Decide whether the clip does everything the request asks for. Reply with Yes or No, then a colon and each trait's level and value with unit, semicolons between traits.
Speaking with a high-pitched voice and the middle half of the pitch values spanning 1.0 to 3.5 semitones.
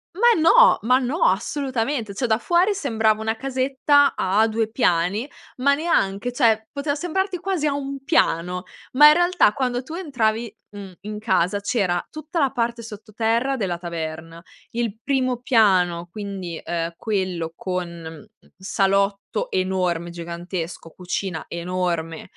No: high, 220 Hz; wide, 6.9 semitones